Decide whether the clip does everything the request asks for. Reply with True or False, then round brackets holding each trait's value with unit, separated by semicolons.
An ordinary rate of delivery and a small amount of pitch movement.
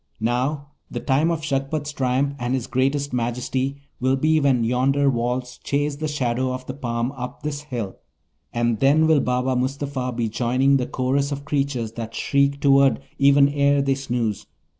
True (170 wpm; 2.1 semitones)